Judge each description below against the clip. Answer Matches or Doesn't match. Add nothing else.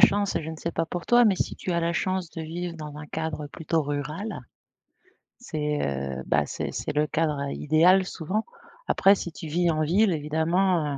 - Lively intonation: Doesn't match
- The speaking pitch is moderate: Matches